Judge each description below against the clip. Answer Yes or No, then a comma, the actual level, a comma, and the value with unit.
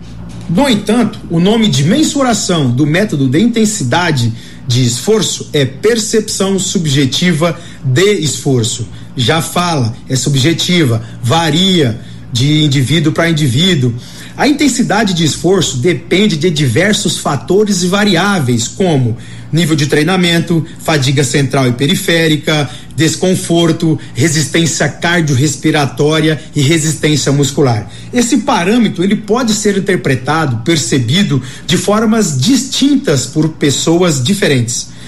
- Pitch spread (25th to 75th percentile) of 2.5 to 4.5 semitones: No, average, 5.2 semitones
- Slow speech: Yes, slow, 110 wpm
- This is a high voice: No, medium, 160 Hz